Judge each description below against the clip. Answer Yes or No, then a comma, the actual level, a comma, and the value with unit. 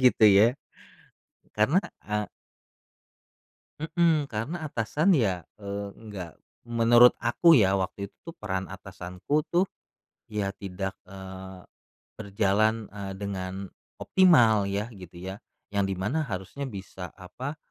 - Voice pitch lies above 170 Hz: No, low, 100 Hz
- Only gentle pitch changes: No, average, 4.1 semitones